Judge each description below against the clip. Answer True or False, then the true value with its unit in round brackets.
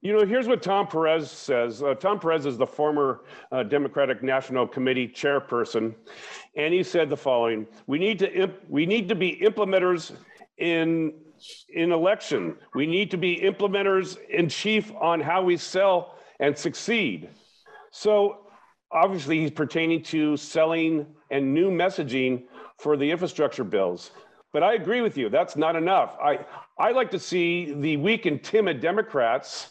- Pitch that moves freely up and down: False (4.8 semitones)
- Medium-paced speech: True (160 wpm)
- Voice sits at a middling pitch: True (165 Hz)